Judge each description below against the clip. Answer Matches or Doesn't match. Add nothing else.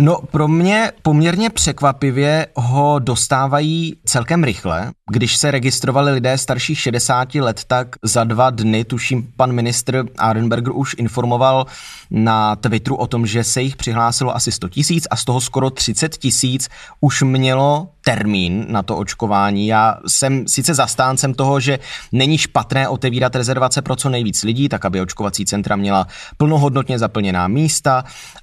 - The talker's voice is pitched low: Matches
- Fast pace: Doesn't match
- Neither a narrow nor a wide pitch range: Matches